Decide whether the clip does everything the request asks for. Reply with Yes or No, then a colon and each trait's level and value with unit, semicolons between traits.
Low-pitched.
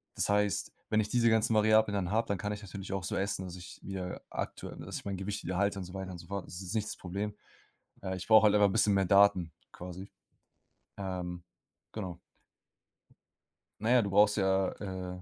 Yes: low, 100 Hz